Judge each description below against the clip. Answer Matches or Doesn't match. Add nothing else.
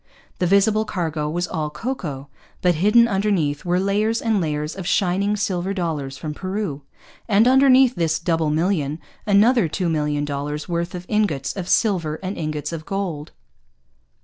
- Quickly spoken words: Doesn't match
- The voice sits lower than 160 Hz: Doesn't match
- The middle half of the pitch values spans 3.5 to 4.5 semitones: Doesn't match